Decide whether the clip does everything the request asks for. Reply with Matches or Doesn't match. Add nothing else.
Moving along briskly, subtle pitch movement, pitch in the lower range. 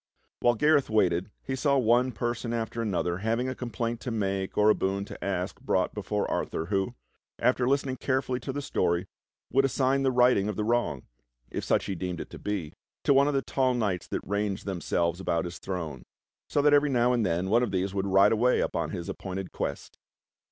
Doesn't match